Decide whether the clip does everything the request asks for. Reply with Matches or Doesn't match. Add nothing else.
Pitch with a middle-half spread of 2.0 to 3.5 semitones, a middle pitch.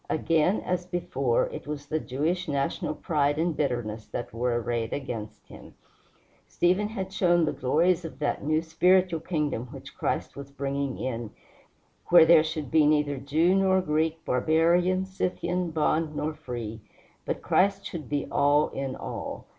Doesn't match